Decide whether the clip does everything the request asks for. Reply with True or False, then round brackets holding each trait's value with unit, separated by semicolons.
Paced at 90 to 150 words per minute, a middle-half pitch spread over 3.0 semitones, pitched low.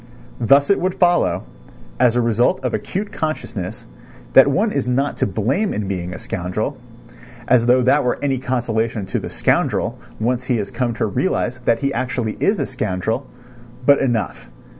False (175 wpm; 3.8 semitones; 125 Hz)